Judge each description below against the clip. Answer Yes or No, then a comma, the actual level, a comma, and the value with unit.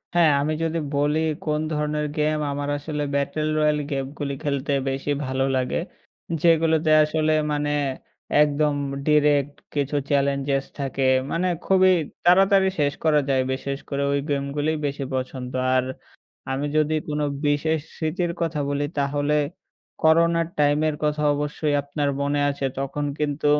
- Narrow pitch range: Yes, narrow, 1.7 semitones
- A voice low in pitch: No, medium, 150 Hz